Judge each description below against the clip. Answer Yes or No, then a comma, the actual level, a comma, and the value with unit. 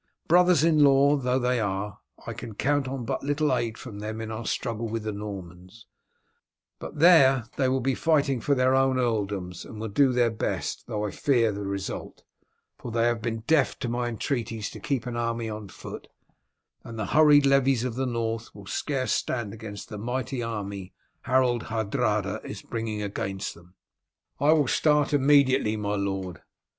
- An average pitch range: Yes, average, 4.0 semitones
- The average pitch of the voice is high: No, low, 115 Hz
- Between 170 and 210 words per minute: Yes, average, 180 wpm